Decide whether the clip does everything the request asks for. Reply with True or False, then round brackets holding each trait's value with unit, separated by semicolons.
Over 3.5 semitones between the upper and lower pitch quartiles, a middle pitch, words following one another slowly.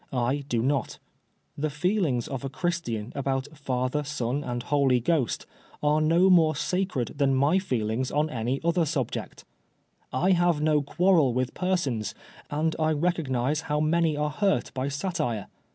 False (4.2 semitones; 145 Hz; 150 wpm)